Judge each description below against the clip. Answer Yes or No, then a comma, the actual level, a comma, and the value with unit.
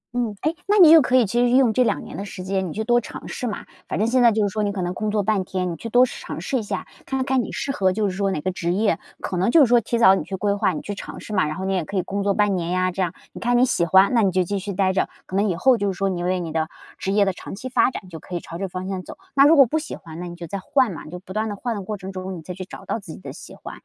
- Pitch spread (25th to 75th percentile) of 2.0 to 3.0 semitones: No, average, 4.0 semitones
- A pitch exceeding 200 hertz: No, high, 195 Hz